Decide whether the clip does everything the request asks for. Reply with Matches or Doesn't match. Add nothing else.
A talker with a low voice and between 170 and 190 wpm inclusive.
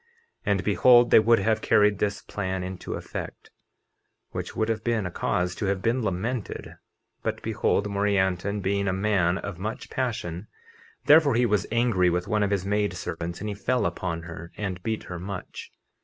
Matches